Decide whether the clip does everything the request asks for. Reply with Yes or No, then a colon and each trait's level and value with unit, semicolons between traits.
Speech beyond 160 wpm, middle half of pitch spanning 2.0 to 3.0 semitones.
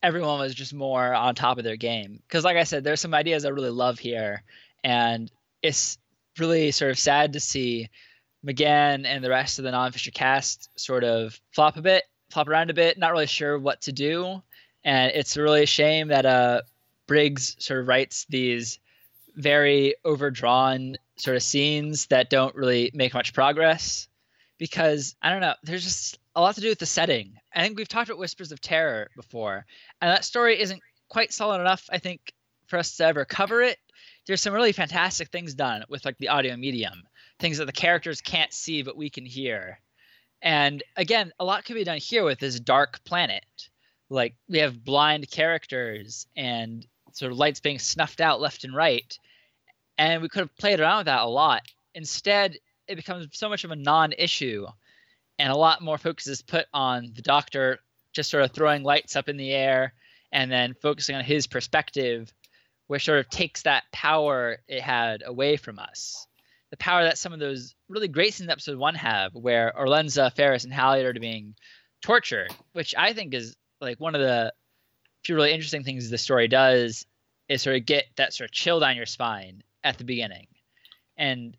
No: average, 195 wpm; average, 4.2 semitones